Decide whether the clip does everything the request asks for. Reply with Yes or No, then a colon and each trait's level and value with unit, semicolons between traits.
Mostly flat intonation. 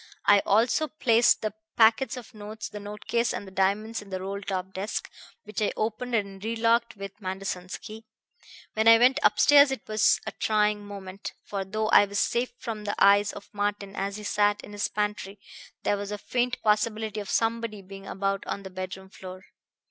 Yes: narrow, 2.1 semitones